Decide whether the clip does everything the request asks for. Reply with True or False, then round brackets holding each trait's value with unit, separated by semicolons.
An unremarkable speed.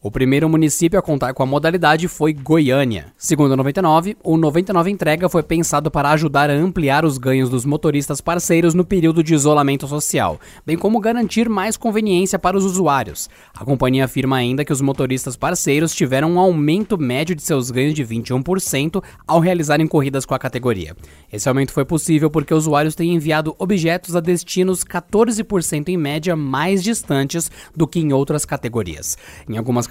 True (175 wpm)